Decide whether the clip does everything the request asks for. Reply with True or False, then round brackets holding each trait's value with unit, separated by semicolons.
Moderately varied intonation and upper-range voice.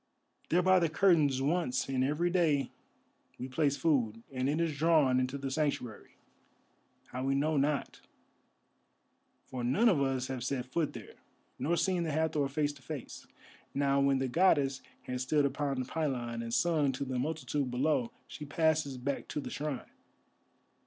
False (3.3 semitones; 140 Hz)